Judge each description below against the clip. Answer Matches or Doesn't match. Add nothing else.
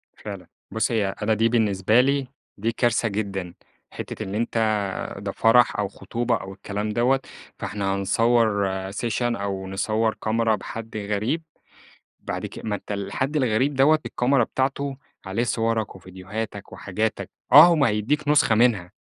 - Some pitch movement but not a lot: Matches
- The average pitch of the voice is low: Matches